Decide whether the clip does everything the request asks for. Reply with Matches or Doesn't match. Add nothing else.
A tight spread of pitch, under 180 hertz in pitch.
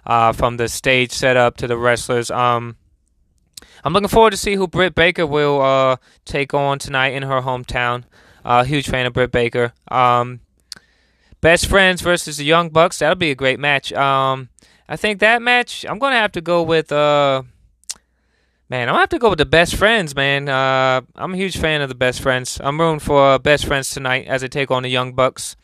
Doesn't match